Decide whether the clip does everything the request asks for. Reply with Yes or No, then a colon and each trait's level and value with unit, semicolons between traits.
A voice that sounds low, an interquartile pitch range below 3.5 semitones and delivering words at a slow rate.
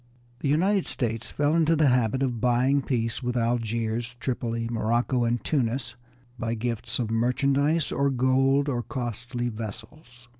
No: low, 120 Hz; average, 2.9 semitones; average, 145 wpm